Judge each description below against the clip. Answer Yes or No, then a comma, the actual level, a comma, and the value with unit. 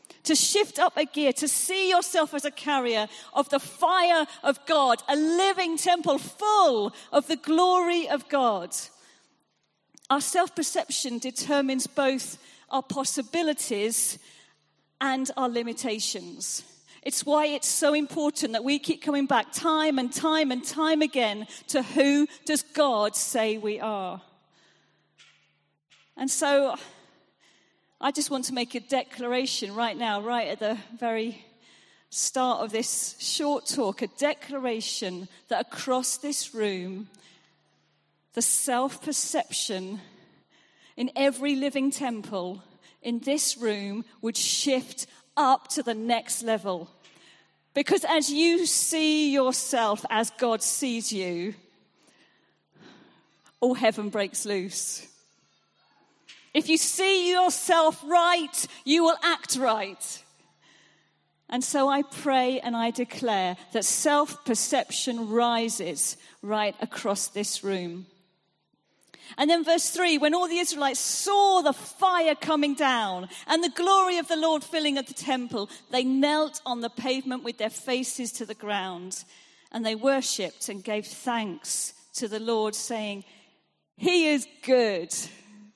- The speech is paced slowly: Yes, slow, 130 wpm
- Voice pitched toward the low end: No, very high, 260 Hz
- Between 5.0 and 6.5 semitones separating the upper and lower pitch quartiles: Yes, wide, 5.5 semitones